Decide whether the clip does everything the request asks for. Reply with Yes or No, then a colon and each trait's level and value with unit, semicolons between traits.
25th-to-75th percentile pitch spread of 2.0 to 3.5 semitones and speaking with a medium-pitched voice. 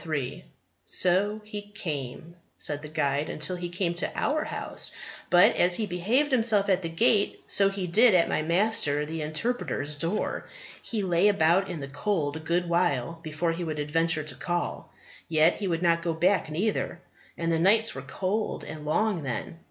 No: average, 4.4 semitones; medium, 175 Hz